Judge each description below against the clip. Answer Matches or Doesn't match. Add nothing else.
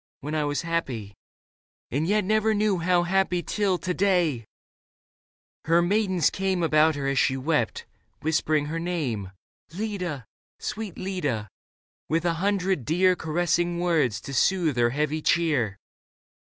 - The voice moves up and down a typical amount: Matches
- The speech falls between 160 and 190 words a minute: Doesn't match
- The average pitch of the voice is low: Doesn't match